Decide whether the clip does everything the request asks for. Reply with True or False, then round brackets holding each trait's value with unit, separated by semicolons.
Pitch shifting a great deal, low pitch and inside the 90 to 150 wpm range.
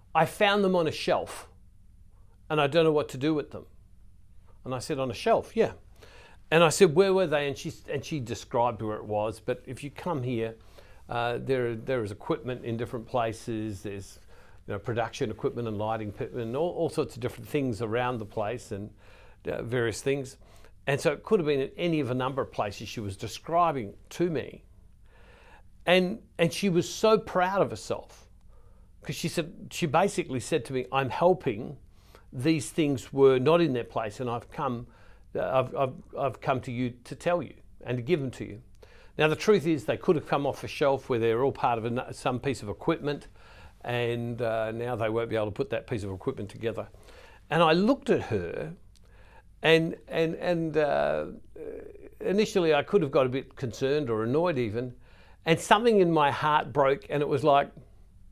False (6.4 semitones; 125 Hz; 200 wpm)